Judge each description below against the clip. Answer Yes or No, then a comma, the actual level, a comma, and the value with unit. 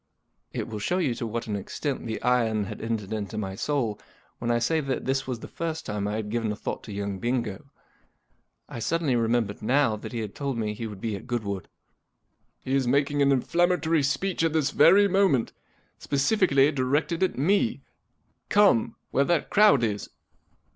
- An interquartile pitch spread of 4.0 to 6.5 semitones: Yes, wide, 5.4 semitones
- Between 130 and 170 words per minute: No, average, 190 wpm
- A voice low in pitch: Yes, low, 125 Hz